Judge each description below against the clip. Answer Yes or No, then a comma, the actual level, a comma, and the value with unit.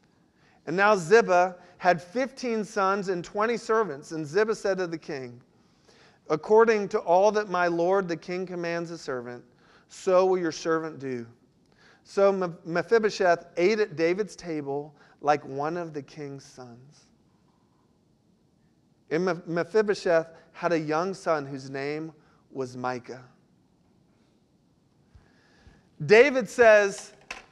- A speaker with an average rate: No, slow, 120 wpm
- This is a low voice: No, medium, 175 Hz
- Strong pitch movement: No, average, 4.7 semitones